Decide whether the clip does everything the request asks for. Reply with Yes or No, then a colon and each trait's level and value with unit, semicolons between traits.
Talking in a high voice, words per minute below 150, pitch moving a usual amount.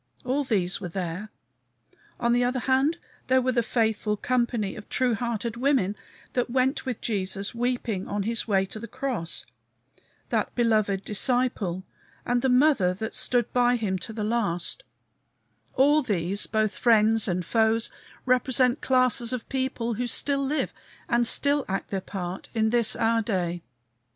No: high, 230 Hz; average, 155 wpm; average, 3.7 semitones